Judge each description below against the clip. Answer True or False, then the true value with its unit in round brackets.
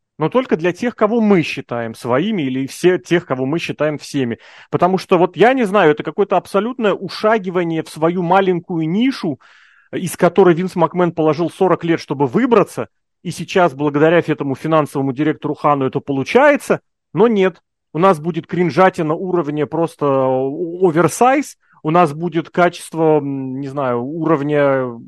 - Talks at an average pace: True (150 wpm)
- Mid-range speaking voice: True (165 Hz)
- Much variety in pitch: False (4.1 semitones)